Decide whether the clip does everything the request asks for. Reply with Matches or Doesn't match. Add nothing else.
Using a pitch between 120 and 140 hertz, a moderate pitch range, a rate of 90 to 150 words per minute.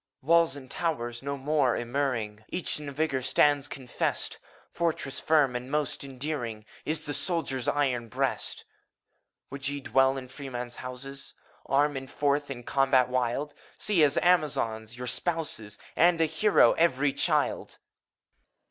Matches